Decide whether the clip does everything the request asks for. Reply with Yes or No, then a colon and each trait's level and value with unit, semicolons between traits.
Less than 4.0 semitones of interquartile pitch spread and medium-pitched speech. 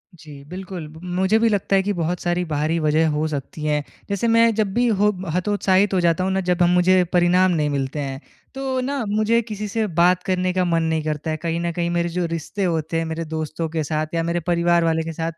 Yes: average, 3.1 semitones; medium, 175 Hz